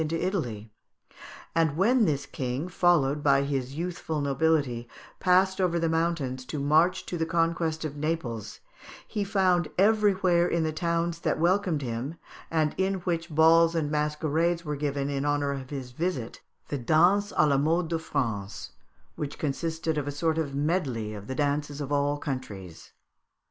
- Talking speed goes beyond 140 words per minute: Yes, average, 165 wpm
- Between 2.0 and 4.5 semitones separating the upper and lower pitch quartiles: Yes, average, 3.4 semitones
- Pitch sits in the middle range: Yes, medium, 155 Hz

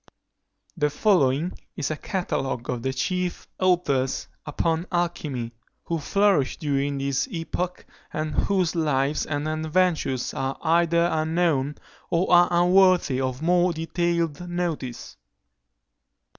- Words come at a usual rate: No, slow, 115 wpm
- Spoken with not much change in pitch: No, average, 4.0 semitones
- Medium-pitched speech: Yes, medium, 160 Hz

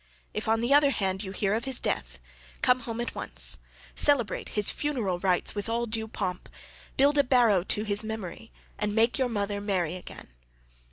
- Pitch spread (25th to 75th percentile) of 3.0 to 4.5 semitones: Yes, average, 3.4 semitones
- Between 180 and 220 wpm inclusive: Yes, average, 185 wpm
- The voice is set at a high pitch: Yes, high, 220 Hz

